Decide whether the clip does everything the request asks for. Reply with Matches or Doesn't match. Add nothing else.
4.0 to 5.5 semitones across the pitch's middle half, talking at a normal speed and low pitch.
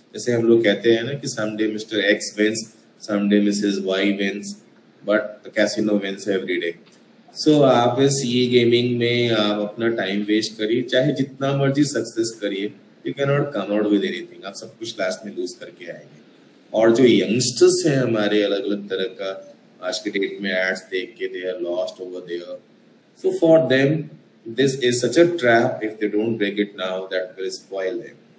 Matches